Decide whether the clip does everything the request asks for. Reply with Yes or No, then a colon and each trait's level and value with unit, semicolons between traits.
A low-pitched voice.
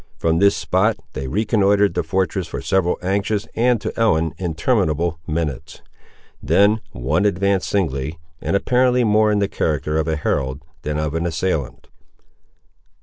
Yes: very low, 90 Hz